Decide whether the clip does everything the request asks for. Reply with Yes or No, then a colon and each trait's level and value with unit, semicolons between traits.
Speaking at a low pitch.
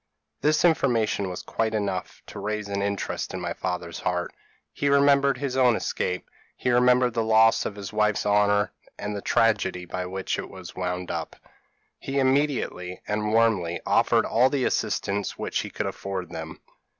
Yes: low, 105 Hz